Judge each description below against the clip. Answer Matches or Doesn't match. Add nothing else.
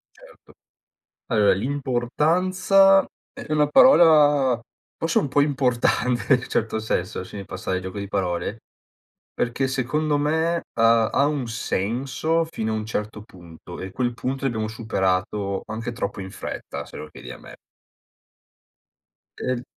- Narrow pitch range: Doesn't match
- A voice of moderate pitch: Doesn't match